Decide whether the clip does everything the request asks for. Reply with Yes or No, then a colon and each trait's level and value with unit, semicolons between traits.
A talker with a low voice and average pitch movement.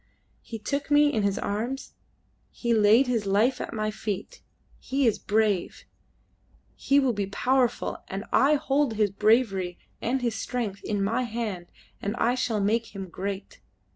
No: high, 220 Hz; average, 3.8 semitones